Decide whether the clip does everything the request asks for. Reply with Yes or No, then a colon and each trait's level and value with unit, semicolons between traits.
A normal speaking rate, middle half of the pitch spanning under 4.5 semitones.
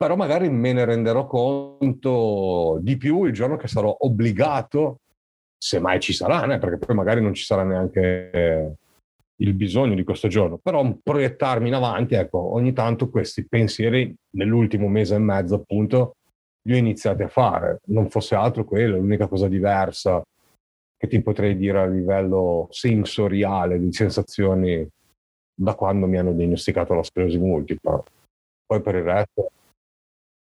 Yes: average, 150 wpm; average, 3.8 semitones